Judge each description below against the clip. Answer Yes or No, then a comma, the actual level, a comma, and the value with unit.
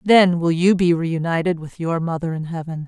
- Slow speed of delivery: No, fast, 210 wpm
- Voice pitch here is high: No, medium, 170 Hz